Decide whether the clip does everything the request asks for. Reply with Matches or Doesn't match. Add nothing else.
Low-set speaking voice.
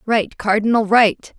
Doesn't match